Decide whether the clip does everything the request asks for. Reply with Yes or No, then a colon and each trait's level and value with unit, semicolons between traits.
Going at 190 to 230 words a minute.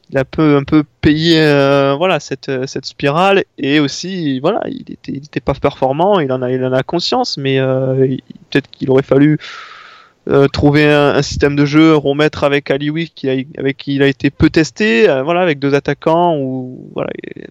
Yes: average, 200 wpm